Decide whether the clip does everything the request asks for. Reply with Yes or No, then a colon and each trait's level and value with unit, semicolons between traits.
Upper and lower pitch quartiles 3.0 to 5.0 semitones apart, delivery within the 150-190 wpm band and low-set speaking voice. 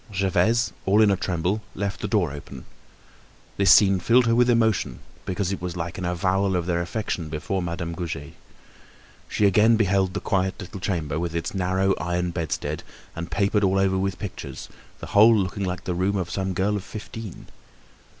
No: narrow, 2.6 semitones; average, 185 wpm; very low, 95 Hz